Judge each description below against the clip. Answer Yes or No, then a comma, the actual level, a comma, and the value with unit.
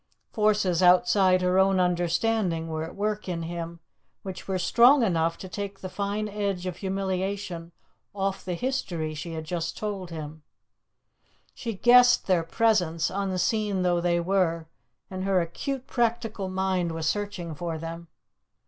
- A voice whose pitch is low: No, medium, 185 Hz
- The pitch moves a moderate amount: Yes, average, 3.2 semitones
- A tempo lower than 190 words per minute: Yes, average, 150 wpm